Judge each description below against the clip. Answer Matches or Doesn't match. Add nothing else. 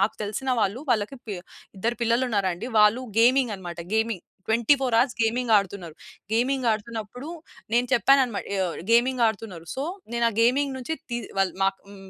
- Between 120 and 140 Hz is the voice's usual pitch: Doesn't match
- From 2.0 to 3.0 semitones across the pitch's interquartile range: Doesn't match